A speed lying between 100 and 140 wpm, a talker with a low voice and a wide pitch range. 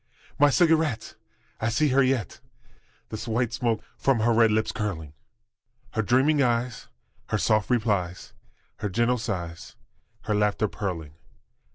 No: slow, 135 wpm; low, 115 Hz; average, 3.1 semitones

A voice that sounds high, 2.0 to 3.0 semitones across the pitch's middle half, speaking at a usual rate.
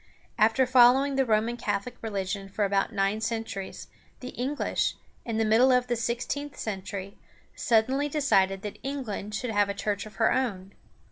No: high, 225 Hz; average, 3.9 semitones; average, 160 wpm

